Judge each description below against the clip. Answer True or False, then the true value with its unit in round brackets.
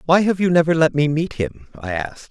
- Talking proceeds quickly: True (260 wpm)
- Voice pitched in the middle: True (150 Hz)